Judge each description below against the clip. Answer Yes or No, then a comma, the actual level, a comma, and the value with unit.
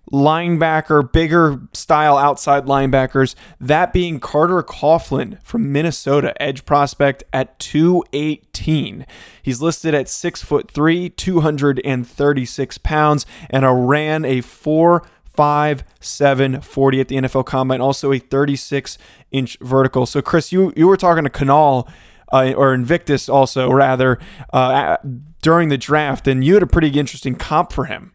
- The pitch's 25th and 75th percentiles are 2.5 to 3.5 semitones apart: Yes, average, 2.9 semitones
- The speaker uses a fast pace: No, average, 140 wpm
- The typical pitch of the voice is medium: Yes, medium, 145 Hz